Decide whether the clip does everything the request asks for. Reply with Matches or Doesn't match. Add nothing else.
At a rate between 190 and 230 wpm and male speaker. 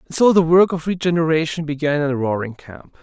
Matches